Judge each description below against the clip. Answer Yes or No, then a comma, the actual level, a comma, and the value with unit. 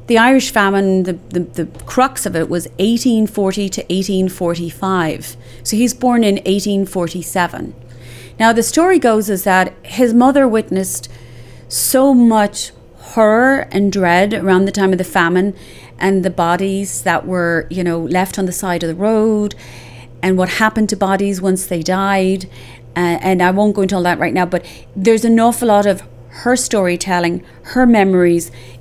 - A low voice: No, high, 190 Hz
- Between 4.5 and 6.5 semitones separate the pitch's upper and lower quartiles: No, average, 3.6 semitones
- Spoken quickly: No, average, 165 wpm